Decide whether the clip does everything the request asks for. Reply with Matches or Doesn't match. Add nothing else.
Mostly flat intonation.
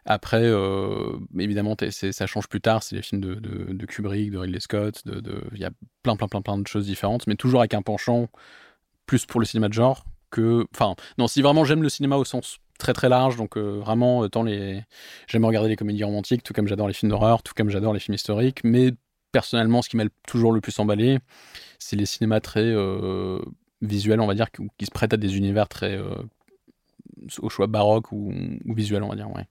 Matches